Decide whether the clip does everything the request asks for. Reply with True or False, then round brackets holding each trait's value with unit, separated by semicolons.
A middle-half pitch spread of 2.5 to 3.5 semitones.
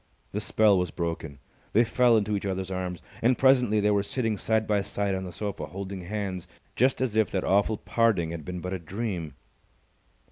True (3.1 semitones)